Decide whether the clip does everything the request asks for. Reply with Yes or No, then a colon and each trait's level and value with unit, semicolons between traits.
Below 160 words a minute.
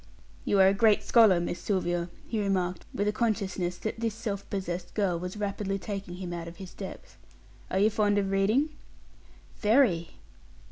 No: average, 175 wpm